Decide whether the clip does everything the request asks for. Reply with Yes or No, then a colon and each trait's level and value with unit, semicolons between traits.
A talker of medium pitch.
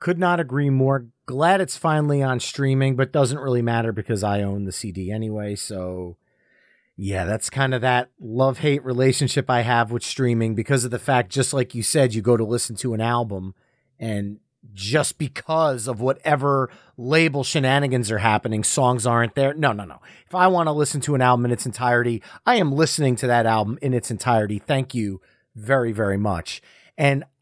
No: low, 125 Hz